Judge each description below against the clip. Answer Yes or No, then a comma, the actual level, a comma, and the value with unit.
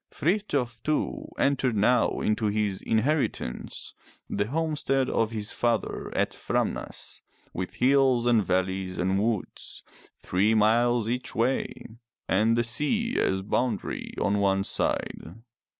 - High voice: No, low, 115 Hz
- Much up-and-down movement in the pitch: No, average, 4.1 semitones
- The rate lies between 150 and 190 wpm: No, slow, 135 wpm